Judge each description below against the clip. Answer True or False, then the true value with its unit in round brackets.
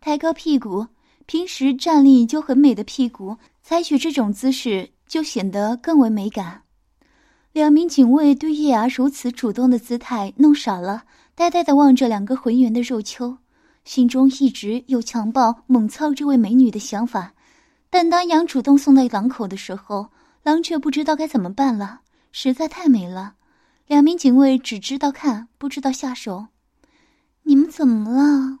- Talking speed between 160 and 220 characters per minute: False (245 characters per minute)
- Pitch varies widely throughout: False (4.4 semitones)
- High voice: True (265 Hz)